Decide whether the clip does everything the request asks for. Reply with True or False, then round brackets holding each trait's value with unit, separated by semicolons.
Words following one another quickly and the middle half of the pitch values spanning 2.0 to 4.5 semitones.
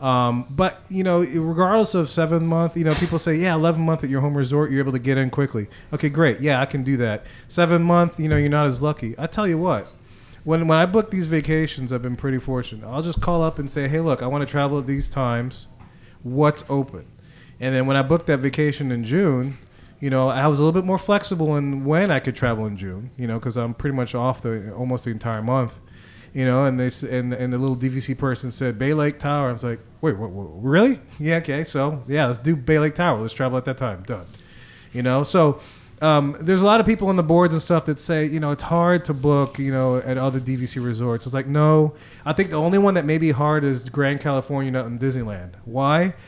True (245 wpm; 4.2 semitones)